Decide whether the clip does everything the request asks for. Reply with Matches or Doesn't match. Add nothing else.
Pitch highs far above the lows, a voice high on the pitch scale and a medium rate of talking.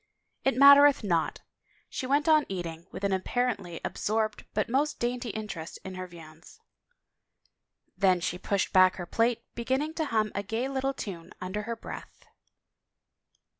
Matches